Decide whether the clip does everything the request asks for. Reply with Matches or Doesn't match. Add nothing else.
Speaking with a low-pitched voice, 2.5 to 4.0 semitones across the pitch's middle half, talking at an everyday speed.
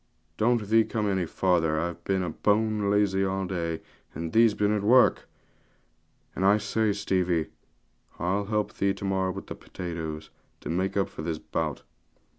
Matches